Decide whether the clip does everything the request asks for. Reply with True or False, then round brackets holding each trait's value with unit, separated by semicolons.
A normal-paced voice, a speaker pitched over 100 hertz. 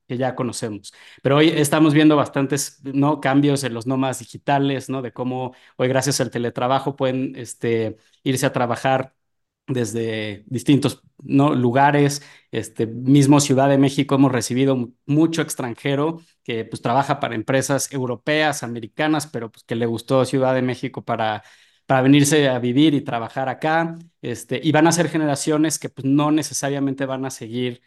True (160 wpm; 135 Hz)